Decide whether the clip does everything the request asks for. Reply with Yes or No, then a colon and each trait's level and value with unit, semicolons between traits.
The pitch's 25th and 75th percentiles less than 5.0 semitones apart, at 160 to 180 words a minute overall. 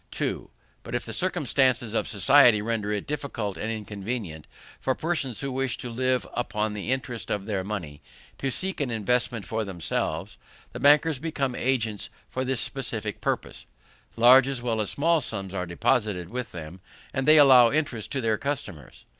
Yes: average, 4.2 semitones; average, 170 wpm